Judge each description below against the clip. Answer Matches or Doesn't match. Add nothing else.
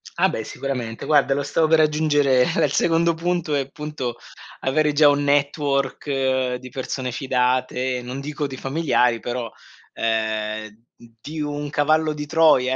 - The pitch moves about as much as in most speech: Matches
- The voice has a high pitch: Doesn't match